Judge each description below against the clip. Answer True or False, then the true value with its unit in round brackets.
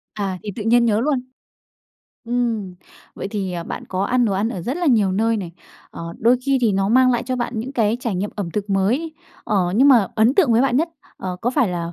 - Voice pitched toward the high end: True (225 Hz)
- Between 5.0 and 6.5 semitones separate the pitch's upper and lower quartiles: False (4.2 semitones)